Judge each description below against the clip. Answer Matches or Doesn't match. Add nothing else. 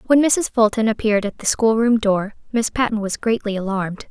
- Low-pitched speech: Doesn't match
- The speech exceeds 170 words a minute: Matches